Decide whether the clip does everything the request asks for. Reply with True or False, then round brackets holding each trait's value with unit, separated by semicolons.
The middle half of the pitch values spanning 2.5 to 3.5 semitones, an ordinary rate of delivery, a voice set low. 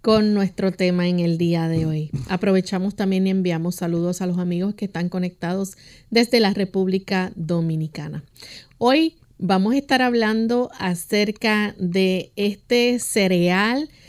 False (3.1 semitones; 135 wpm; 190 Hz)